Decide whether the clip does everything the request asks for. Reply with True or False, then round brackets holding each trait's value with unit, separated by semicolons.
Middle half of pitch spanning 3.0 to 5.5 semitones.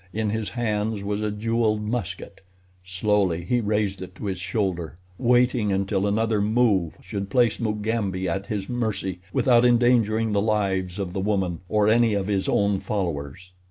False (2.6 semitones)